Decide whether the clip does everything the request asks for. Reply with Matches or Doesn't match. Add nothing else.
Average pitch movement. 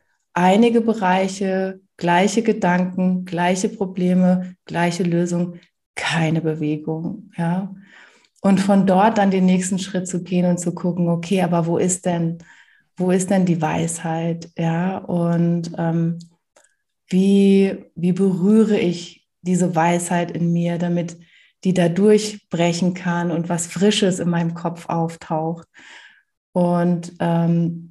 Doesn't match